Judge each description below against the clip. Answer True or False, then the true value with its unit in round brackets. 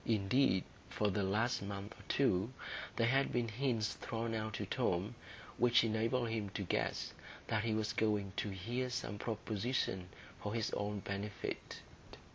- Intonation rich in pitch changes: False (2.6 semitones)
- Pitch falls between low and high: False (110 Hz)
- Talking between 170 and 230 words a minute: False (155 wpm)